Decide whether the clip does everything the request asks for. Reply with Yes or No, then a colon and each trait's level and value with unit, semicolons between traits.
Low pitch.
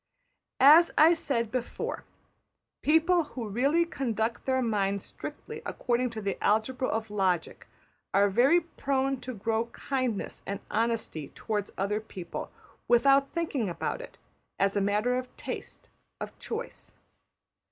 No: high, 235 Hz